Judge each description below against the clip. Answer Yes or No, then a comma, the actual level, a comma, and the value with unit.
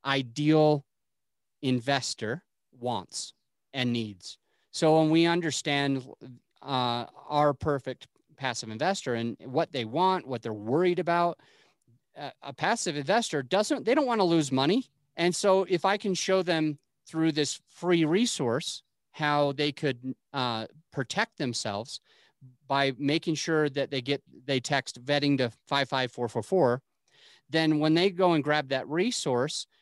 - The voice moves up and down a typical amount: Yes, average, 4.5 semitones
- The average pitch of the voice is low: No, medium, 145 Hz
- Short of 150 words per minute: Yes, average, 140 wpm